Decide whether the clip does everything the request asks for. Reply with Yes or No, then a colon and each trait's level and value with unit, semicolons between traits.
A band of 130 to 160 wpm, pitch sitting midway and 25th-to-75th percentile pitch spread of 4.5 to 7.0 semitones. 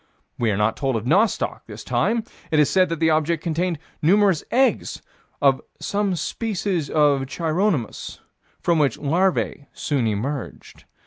Yes: average, 145 wpm; medium, 155 Hz; average, 5.0 semitones